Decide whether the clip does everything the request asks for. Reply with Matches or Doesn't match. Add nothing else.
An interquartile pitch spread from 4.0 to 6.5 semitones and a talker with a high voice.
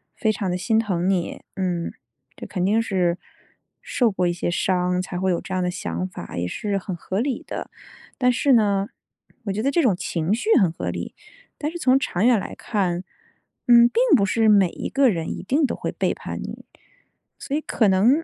Matches